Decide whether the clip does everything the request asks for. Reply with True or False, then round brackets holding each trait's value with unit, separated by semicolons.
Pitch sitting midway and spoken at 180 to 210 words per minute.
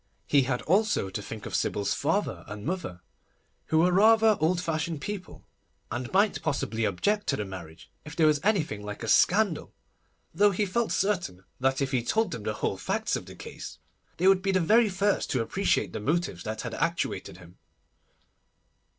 True (160 Hz; 185 wpm)